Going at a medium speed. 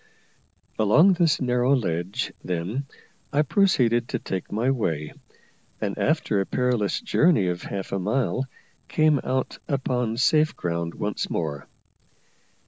No: slow, 130 wpm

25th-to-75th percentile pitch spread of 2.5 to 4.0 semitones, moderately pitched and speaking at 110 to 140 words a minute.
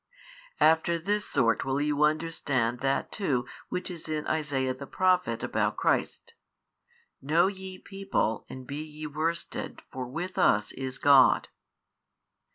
No: average, 4.6 semitones; medium, 150 Hz; slow, 135 wpm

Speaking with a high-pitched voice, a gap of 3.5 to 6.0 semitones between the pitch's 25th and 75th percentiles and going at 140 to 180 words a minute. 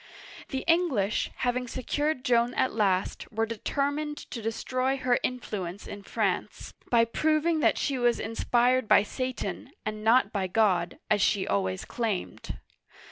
Yes: high, 235 Hz; average, 3.8 semitones; average, 145 wpm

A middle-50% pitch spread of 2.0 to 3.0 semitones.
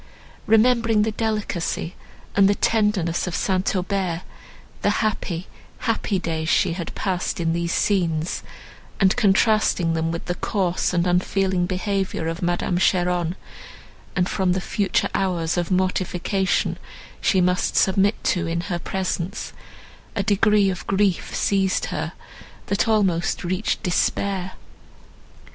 Yes: narrow, 2.5 semitones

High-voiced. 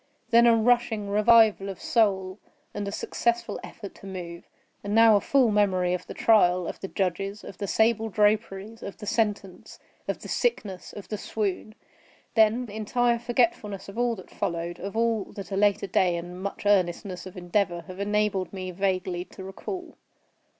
Yes: high, 200 Hz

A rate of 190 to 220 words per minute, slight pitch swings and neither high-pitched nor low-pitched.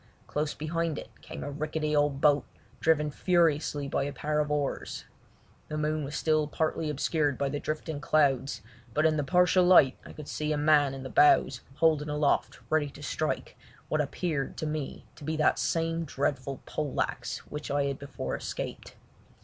No: average, 180 wpm; narrow, 1.5 semitones; medium, 150 Hz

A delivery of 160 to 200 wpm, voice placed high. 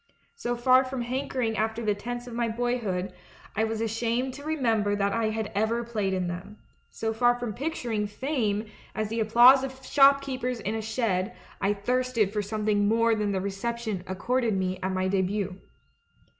Yes: average, 175 wpm; high, 225 Hz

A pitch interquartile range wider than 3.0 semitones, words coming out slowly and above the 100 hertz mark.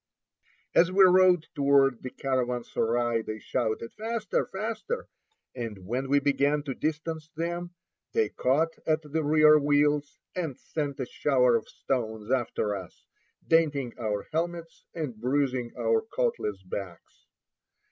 Yes: average, 5.2 semitones; slow, 130 wpm; medium, 140 Hz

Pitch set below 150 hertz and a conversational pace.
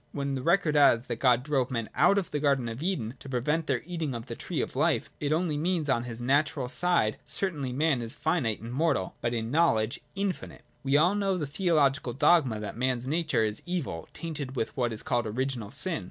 No: medium, 140 Hz; fast, 220 wpm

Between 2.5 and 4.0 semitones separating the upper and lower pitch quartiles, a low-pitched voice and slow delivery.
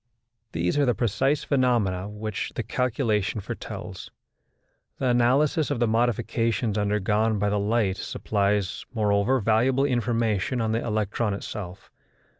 Yes: average, 3.0 semitones; low, 110 Hz; slow, 125 wpm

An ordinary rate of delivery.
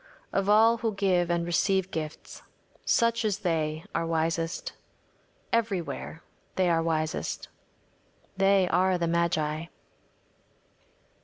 No: slow, 105 wpm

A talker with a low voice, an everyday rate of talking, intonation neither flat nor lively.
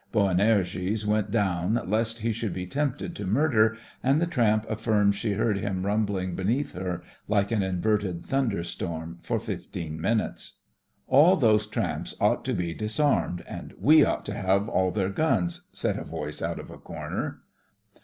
Yes: low, 105 Hz; average, 165 wpm; average, 3.6 semitones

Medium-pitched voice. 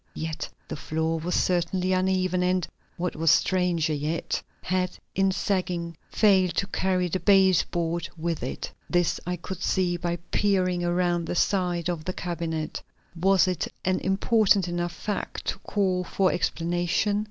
Yes: medium, 180 Hz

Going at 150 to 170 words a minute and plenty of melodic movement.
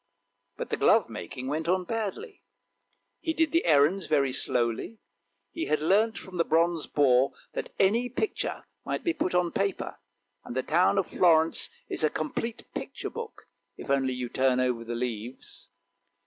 Yes: average, 160 wpm; wide, 7.2 semitones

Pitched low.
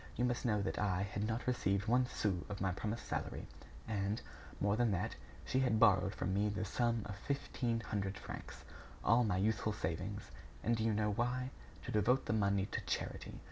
Yes: low, 105 Hz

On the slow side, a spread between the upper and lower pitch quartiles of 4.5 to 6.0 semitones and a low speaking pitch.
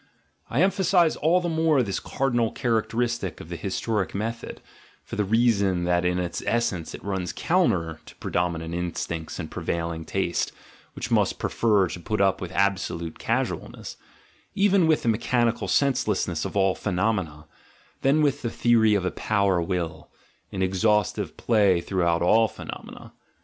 No: average, 155 wpm; average, 5.0 semitones; low, 100 Hz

